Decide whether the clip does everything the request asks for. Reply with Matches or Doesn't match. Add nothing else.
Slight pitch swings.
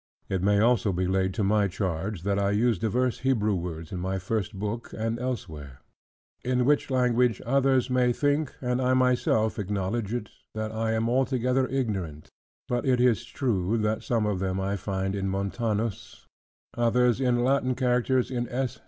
Doesn't match